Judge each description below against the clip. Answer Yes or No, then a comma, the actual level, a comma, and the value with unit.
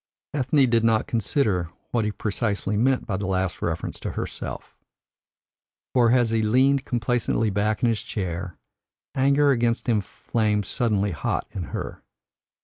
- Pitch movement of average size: Yes, average, 3.3 semitones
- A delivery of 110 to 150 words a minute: Yes, average, 145 wpm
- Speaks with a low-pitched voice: Yes, low, 110 Hz